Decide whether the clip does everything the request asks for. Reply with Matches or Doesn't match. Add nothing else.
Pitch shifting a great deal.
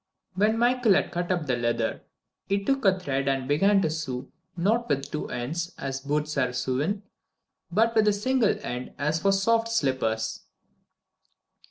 Matches